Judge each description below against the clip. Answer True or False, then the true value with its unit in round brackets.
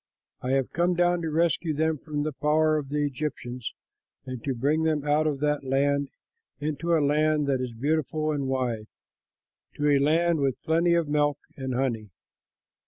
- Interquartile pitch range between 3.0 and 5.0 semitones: False (2.6 semitones)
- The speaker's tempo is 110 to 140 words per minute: False (175 wpm)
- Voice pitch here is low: False (150 Hz)